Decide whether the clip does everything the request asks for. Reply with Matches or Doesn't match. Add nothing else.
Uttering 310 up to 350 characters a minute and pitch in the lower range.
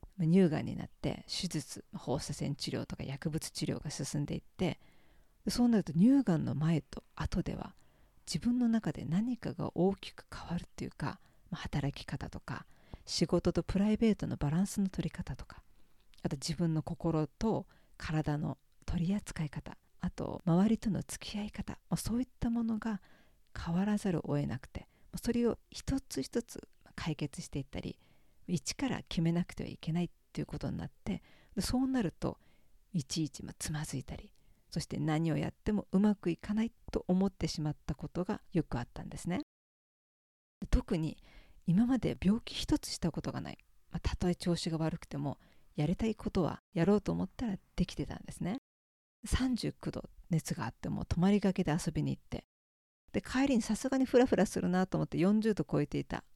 Doesn't match